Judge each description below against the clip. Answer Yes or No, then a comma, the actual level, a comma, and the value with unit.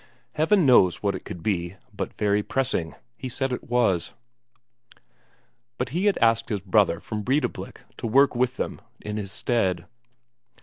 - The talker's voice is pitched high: No, low, 115 Hz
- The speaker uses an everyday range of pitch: Yes, average, 5.0 semitones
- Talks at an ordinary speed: Yes, average, 160 wpm